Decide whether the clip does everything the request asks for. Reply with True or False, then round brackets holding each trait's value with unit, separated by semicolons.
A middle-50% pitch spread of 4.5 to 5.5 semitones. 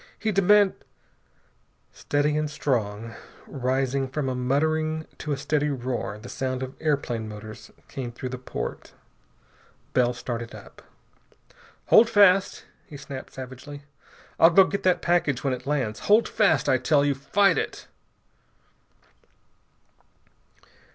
False (3.8 semitones)